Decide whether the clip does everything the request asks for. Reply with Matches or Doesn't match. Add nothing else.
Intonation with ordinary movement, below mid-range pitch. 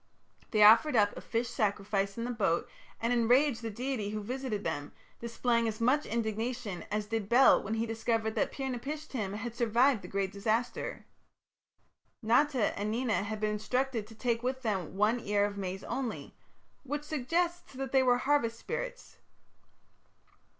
Doesn't match